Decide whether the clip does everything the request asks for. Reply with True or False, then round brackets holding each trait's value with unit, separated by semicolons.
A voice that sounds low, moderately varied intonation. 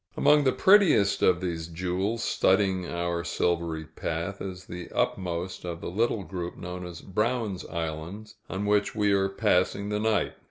True (95 Hz; 3.1 semitones)